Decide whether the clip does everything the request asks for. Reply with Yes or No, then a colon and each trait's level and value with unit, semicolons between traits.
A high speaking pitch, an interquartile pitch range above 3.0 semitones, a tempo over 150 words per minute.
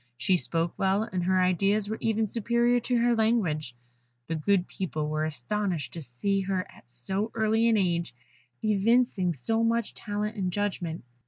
Yes: high, 195 Hz; average, 4.5 semitones; average, 165 wpm